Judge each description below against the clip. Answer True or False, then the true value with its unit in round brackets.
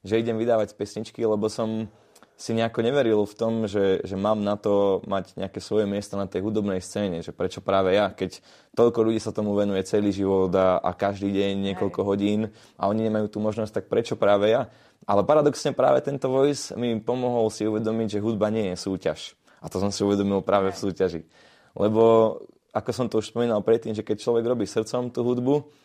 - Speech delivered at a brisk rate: True (200 wpm)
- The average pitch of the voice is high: False (105 Hz)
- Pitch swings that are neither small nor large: False (2.2 semitones)